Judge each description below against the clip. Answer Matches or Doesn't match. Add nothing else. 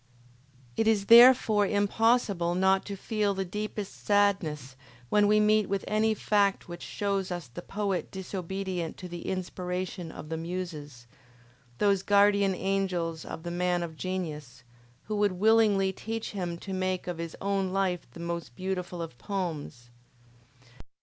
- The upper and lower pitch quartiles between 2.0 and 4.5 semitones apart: Matches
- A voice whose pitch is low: Doesn't match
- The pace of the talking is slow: Doesn't match